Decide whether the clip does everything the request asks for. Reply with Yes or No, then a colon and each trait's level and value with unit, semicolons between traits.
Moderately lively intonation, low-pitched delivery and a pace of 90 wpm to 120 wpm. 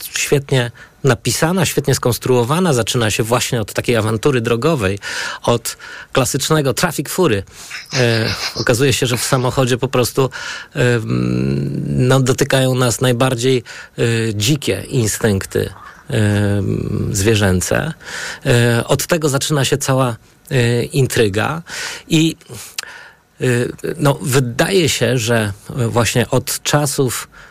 Yes: average, 3.4 semitones; low, 125 Hz; slow, 110 wpm